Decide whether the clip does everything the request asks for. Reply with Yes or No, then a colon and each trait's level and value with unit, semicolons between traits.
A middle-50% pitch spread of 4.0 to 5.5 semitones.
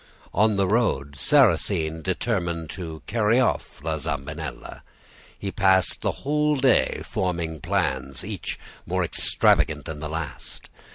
Yes: average, 5.1 semitones